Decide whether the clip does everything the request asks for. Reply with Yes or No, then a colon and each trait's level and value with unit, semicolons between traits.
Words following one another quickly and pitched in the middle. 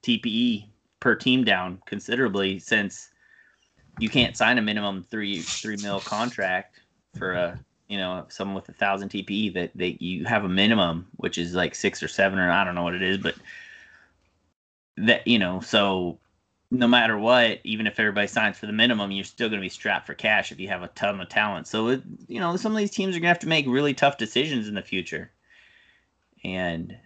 No: fast, 215 wpm; low, 100 Hz